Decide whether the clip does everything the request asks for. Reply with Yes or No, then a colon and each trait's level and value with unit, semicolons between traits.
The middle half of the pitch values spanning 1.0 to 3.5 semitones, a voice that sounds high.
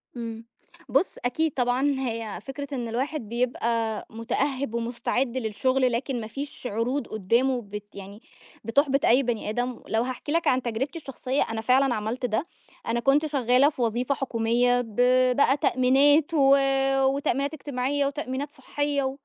Yes: average, 3.1 semitones; very high, 250 Hz